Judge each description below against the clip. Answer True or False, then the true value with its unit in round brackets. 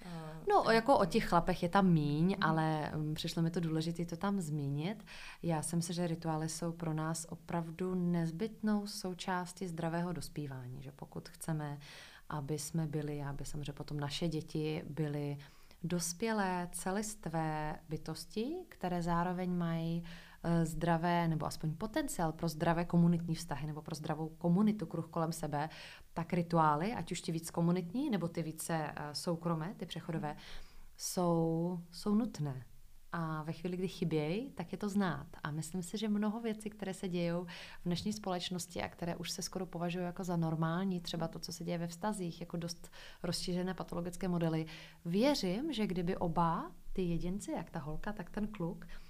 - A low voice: False (170 Hz)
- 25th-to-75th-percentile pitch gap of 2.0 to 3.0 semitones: True (2.5 semitones)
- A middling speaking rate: True (160 wpm)